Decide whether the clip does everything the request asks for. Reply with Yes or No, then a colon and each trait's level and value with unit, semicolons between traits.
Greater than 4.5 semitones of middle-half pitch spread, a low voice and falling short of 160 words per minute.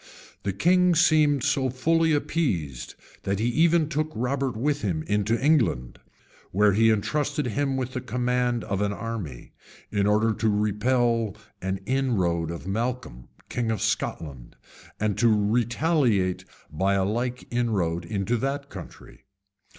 Yes: average, 5.2 semitones; low, 115 Hz; average, 140 wpm